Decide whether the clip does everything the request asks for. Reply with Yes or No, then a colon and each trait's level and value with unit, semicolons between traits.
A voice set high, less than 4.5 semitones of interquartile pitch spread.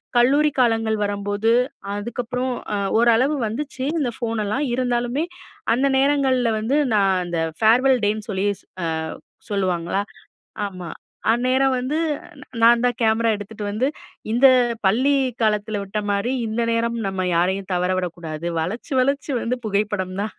Yes: high, 225 Hz; average, 4.0 semitones